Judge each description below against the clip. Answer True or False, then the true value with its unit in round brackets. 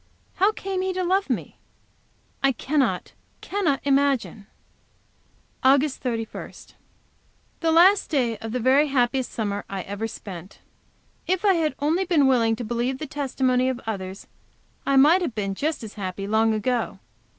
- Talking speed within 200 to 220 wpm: False (150 wpm)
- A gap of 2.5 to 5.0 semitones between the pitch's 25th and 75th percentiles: False (5.5 semitones)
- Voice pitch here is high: True (260 Hz)